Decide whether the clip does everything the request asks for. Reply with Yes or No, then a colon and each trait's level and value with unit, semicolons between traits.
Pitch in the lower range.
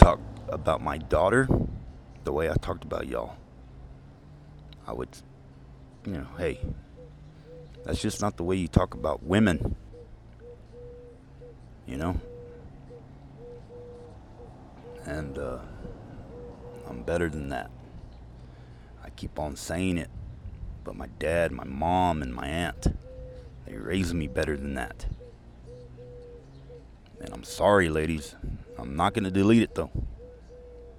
Yes: very low, 85 Hz